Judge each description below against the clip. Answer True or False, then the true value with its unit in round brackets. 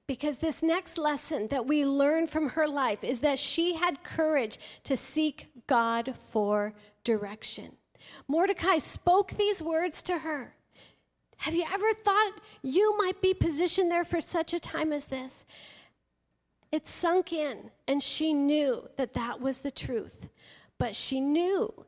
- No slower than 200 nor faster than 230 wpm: False (150 wpm)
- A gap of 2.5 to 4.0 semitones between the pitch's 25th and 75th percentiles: False (4.7 semitones)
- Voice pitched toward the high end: True (310 Hz)